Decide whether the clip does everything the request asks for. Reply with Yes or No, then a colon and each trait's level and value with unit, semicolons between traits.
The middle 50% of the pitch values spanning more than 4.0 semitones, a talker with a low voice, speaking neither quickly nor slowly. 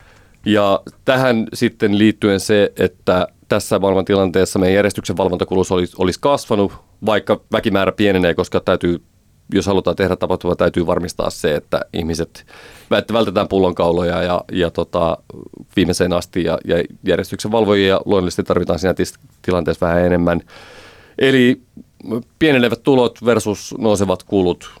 No: average, 3.1 semitones; low, 100 Hz; average, 125 wpm